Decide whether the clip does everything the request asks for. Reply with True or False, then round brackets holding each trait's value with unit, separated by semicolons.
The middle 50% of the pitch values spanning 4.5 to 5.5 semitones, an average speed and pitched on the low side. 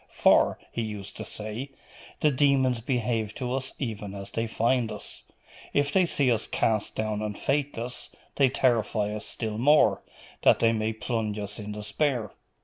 False (3.5 semitones; 165 wpm; 115 Hz)